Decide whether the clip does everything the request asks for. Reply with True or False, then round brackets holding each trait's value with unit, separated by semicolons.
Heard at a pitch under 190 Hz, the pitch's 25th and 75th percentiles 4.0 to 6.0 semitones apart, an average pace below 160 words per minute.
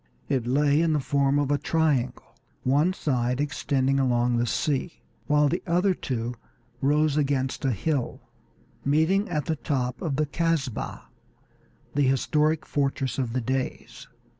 False (140 Hz; 2.8 semitones; 145 wpm)